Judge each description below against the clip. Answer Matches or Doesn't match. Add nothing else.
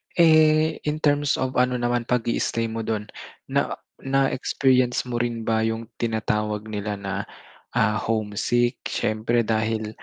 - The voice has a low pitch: Matches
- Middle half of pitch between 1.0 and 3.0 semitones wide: Matches